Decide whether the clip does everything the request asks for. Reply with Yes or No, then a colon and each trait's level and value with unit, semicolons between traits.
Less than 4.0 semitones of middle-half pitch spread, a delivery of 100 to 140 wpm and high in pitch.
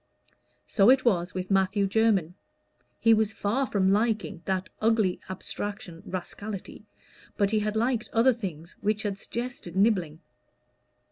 Yes: average, 3.1 semitones; slow, 135 wpm; high, 205 Hz